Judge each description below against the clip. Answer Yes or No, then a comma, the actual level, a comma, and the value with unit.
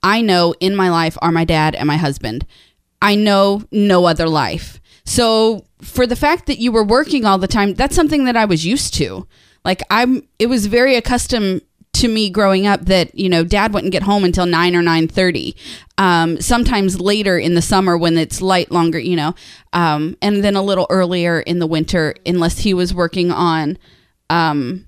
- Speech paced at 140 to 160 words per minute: No, average, 200 wpm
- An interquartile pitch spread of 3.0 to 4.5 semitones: Yes, average, 3.7 semitones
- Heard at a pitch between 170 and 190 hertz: Yes, medium, 185 Hz